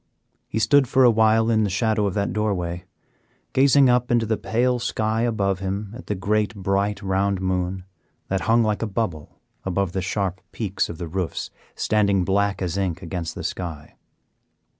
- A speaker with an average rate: Yes, average, 180 wpm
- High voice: No, low, 100 Hz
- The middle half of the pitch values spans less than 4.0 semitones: Yes, average, 2.9 semitones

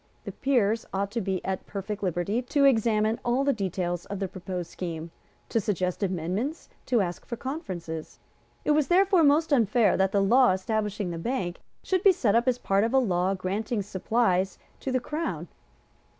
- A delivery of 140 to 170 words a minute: No, average, 180 wpm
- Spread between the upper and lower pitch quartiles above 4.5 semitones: Yes, average, 5.2 semitones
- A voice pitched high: Yes, high, 210 Hz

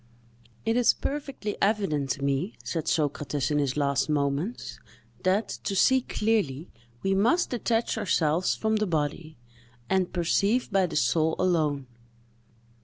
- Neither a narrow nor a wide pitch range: No, wide, 6.3 semitones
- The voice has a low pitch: No, medium, 175 Hz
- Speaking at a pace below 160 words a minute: Yes, slow, 135 wpm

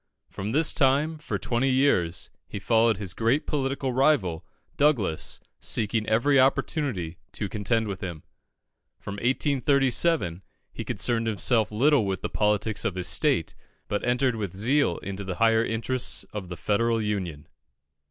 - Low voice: Yes, low, 115 Hz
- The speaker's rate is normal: Yes, average, 145 wpm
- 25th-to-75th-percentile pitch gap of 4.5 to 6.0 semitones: Yes, average, 5.1 semitones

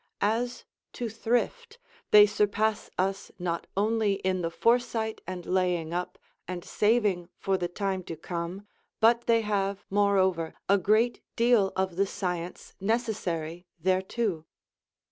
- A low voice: No, high, 195 Hz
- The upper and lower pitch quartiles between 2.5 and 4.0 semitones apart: Yes, average, 3.5 semitones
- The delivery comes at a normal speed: No, slow, 130 wpm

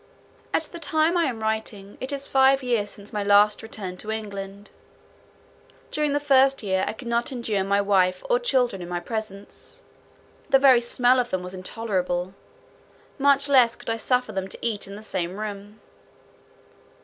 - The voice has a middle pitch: No, high, 220 Hz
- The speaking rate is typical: Yes, average, 175 wpm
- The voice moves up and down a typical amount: Yes, average, 4.7 semitones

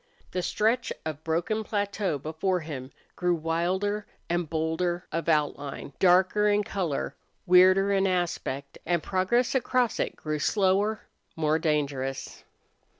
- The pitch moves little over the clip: No, average, 4.2 semitones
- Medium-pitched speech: Yes, medium, 175 Hz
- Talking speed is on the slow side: Yes, slow, 125 wpm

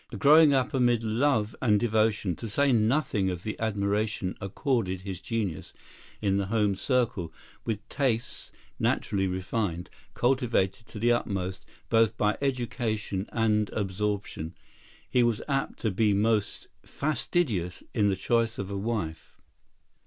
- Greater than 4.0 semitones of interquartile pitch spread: No, average, 3.4 semitones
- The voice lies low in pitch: Yes, low, 110 Hz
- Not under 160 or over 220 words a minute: No, slow, 135 wpm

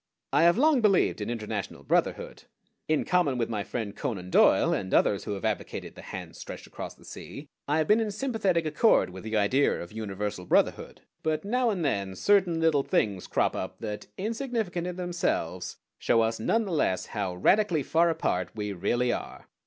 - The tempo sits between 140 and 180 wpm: No, average, 190 wpm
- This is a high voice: No, medium, 140 Hz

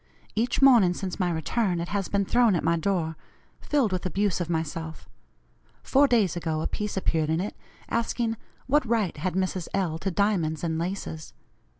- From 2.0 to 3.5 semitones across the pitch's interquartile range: No, average, 4.4 semitones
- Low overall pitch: No, medium, 185 Hz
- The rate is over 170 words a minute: Yes, average, 180 wpm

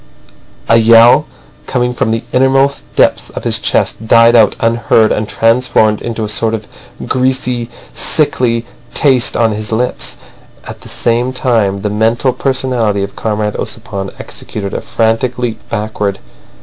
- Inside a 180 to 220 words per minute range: No, average, 145 wpm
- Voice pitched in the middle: No, low, 115 Hz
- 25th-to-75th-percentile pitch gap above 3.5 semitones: No, narrow, 2.5 semitones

